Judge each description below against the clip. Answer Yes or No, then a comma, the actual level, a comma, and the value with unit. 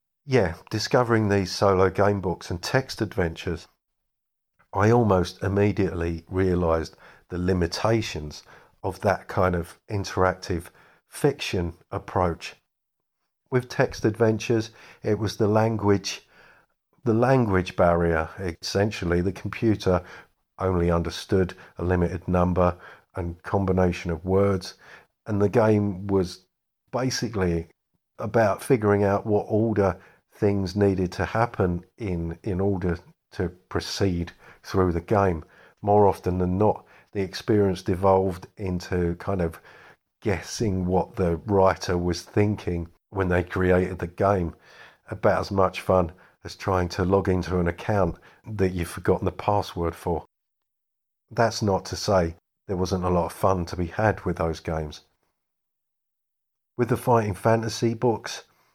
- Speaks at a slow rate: Yes, slow, 130 wpm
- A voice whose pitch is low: Yes, very low, 95 Hz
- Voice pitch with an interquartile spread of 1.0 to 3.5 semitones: Yes, average, 2.8 semitones